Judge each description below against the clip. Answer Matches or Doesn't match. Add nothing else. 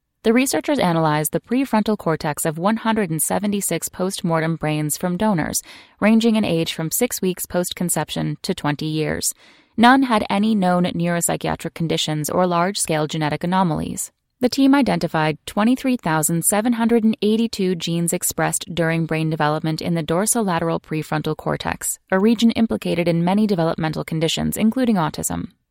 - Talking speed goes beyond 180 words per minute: Doesn't match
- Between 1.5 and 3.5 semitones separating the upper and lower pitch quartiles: Doesn't match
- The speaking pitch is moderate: Matches